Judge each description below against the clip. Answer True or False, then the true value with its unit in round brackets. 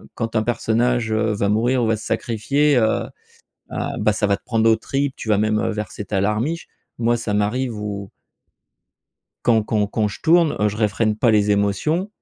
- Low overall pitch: True (110 Hz)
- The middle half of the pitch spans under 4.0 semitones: True (2.4 semitones)